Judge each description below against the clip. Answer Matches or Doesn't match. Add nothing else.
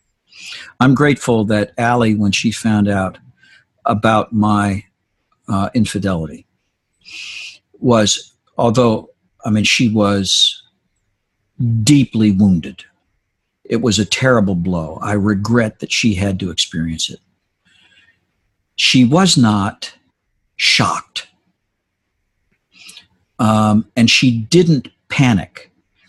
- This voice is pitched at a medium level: Doesn't match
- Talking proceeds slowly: Matches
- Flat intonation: Doesn't match